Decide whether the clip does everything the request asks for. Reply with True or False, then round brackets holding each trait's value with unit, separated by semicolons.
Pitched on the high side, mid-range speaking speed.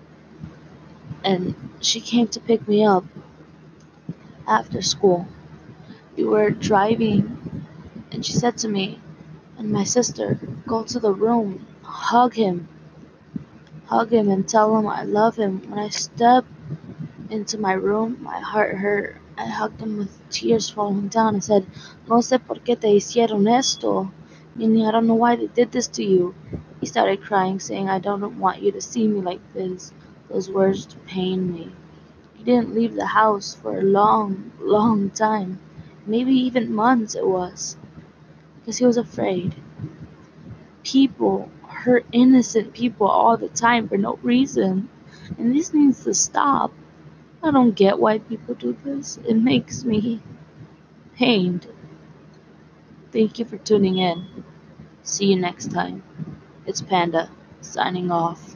True (210 Hz; 150 wpm)